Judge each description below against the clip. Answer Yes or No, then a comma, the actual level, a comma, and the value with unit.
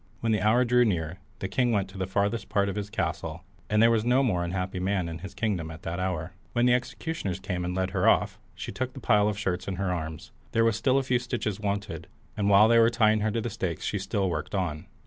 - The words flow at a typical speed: No, fast, 260 wpm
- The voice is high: No, low, 100 Hz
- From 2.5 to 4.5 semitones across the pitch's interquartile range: Yes, average, 3.9 semitones